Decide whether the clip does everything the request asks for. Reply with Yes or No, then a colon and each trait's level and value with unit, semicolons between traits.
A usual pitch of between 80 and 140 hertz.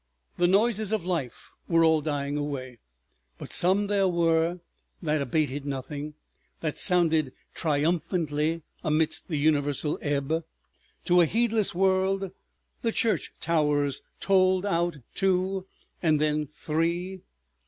No: medium, 165 Hz